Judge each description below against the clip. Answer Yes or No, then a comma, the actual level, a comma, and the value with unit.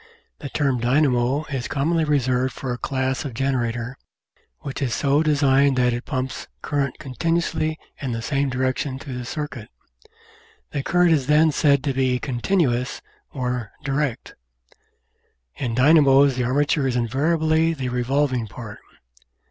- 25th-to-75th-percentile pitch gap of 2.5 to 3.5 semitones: Yes, average, 2.9 semitones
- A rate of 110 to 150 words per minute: Yes, average, 145 wpm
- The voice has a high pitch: No, low, 135 Hz